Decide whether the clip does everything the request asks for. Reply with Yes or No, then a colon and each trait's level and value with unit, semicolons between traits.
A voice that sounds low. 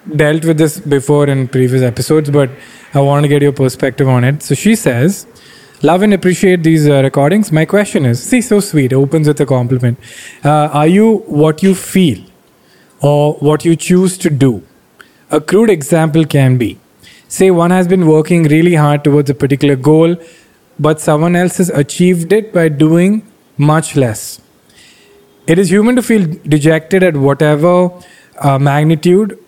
No: medium, 155 Hz